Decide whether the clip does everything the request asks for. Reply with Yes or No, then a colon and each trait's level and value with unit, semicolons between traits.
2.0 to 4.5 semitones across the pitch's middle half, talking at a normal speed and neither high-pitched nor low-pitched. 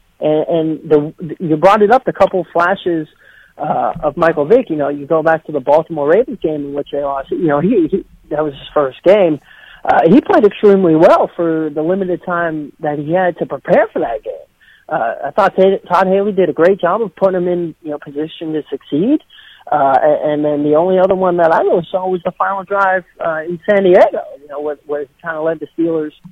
No: average, 3.6 semitones; fast, 220 wpm; medium, 165 Hz